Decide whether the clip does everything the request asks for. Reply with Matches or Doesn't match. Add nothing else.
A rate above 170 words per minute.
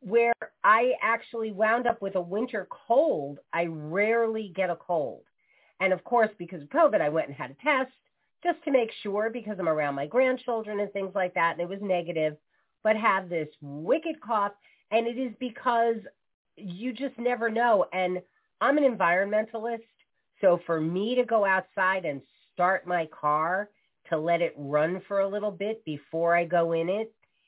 Matches